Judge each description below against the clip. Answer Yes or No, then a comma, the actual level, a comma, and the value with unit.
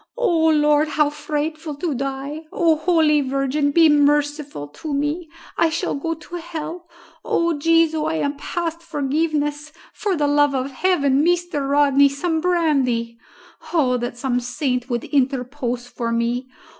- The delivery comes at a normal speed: Yes, average, 145 wpm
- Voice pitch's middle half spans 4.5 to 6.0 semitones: No, average, 2.9 semitones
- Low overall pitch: No, very high, 295 Hz